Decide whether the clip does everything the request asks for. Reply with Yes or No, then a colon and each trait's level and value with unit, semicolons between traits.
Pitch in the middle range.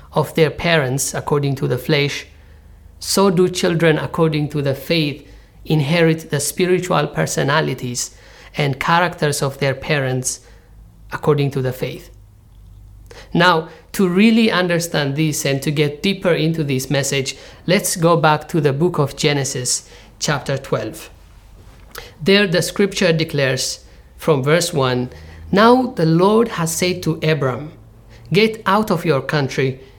Yes: medium, 150 Hz